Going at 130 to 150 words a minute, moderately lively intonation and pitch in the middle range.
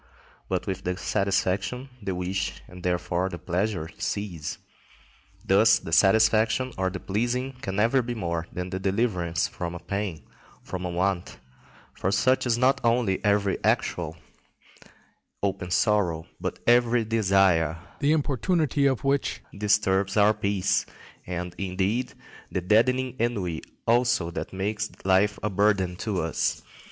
No: average, 140 wpm; average, 3.9 semitones; low, 100 Hz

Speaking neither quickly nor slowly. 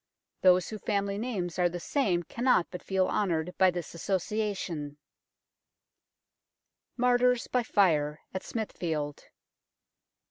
No: slow, 110 wpm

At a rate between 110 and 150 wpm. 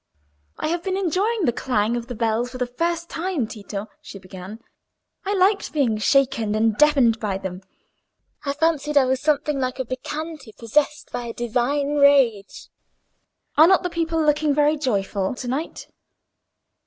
No: average, 165 wpm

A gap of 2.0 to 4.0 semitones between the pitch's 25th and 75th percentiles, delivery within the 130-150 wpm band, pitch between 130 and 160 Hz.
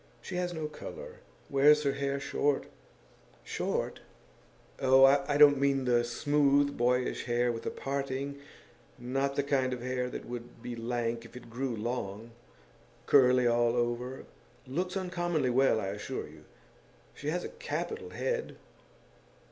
Yes: average, 3.0 semitones; average, 145 wpm; low, 135 Hz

